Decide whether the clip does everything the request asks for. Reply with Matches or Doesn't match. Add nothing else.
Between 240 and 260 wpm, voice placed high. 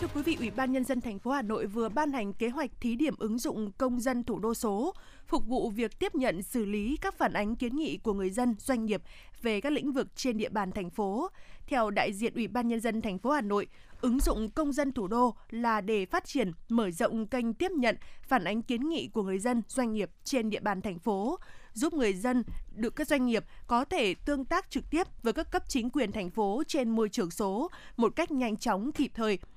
Matches